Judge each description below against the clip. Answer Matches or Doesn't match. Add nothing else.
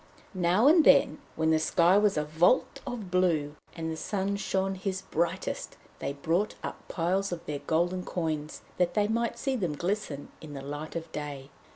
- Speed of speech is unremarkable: Matches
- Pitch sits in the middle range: Matches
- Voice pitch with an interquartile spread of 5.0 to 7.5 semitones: Doesn't match